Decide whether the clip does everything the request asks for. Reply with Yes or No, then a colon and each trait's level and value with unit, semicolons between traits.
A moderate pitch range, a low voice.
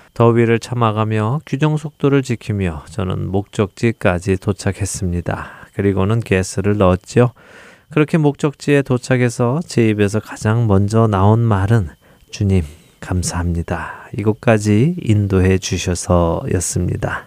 Yes: average, 4.2 semitones; low, 110 Hz